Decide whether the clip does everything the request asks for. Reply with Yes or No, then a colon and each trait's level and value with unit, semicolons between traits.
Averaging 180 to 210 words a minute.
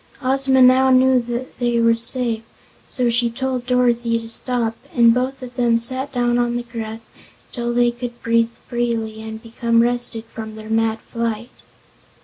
No: average, 160 wpm